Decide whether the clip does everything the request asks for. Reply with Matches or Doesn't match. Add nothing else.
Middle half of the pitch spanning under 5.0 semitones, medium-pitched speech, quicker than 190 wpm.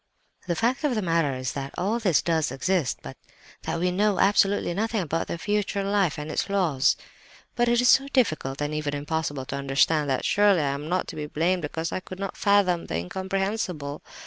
Doesn't match